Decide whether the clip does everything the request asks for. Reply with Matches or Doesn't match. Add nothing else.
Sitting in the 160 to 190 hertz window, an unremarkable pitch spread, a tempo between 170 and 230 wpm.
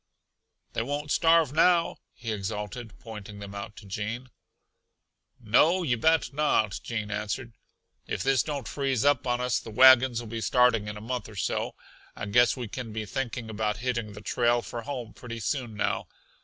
Doesn't match